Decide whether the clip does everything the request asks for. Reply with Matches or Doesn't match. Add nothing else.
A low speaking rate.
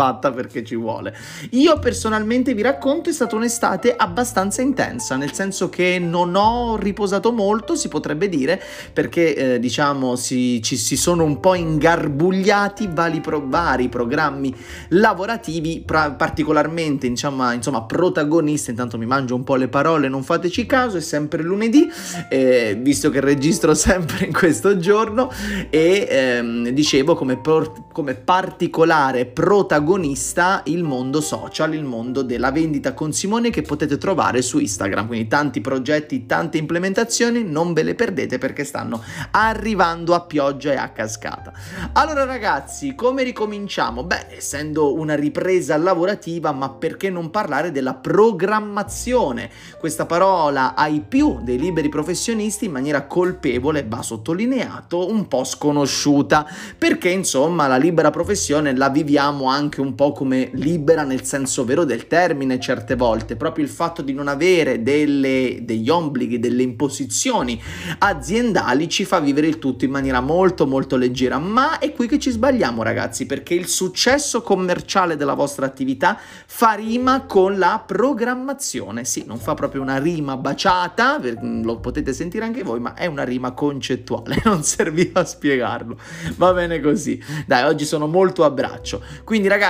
Doesn't match